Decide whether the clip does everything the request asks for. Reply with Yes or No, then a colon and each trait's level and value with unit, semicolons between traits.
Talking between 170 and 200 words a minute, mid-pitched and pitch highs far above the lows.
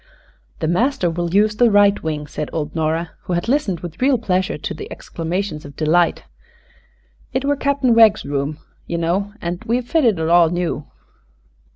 Yes: average, 175 wpm; medium, 180 Hz; wide, 5.8 semitones